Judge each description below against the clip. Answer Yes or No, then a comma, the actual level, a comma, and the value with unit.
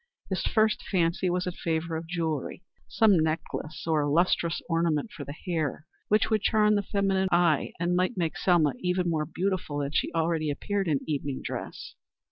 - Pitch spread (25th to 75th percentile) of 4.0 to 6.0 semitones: No, average, 3.1 semitones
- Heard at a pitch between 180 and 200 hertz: No, medium, 170 Hz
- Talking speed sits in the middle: Yes, average, 175 wpm